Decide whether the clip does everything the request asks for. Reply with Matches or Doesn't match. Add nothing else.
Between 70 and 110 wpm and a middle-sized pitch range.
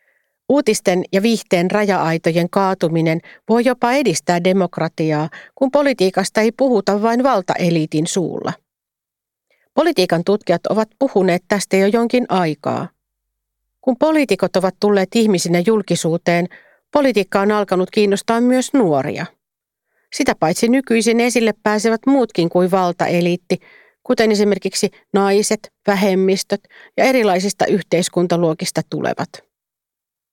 Matches